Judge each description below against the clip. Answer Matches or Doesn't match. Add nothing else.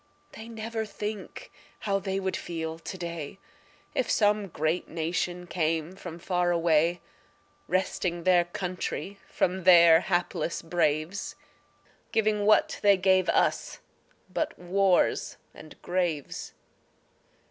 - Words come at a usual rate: Doesn't match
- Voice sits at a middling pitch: Matches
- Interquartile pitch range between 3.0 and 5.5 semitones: Doesn't match